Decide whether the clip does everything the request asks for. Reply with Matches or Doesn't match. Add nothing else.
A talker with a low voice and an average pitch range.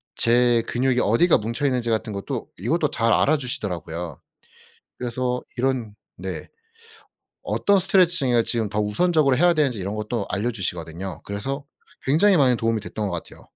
Matches